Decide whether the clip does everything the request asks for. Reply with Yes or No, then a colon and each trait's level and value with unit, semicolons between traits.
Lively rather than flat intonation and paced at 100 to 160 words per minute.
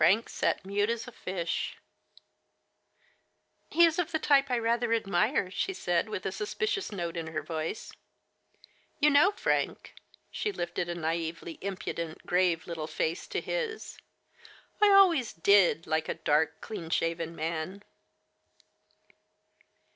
Yes: wide, 7.3 semitones; average, 140 wpm